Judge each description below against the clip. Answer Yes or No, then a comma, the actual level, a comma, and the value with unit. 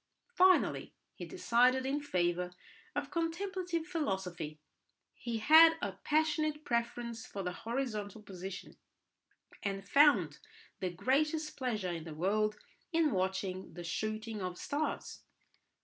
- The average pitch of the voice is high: Yes, high, 230 Hz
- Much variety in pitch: Yes, wide, 8.3 semitones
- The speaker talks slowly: Yes, slow, 115 wpm